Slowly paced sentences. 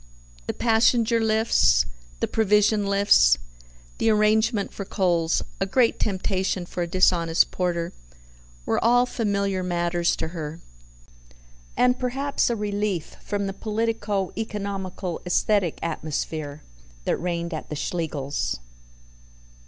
Yes: slow, 115 wpm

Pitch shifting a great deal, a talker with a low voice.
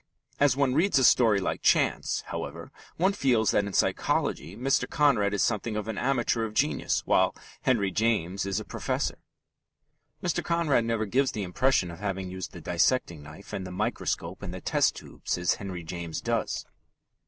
Yes: wide, 5.7 semitones; low, 105 Hz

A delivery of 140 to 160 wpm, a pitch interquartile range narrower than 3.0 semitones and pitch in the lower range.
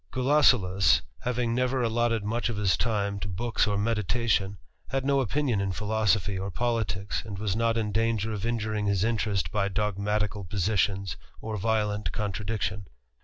Yes: average, 155 wpm; narrow, 2.6 semitones; low, 105 Hz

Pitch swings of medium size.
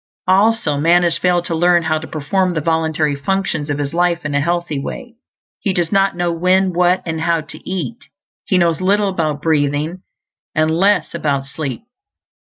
Yes: average, 3.0 semitones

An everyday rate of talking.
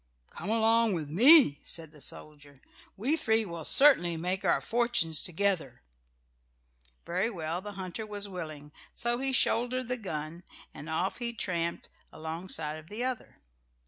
Yes: average, 145 wpm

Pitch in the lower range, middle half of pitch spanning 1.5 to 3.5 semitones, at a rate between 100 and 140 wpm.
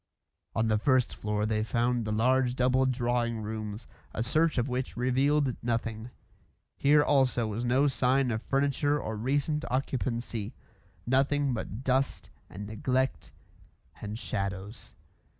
Yes: low, 125 Hz; average, 3.2 semitones; slow, 135 wpm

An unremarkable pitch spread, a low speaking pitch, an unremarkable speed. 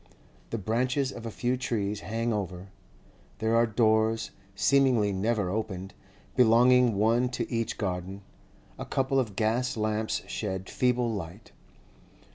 No: average, 3.1 semitones; low, 110 Hz; slow, 130 wpm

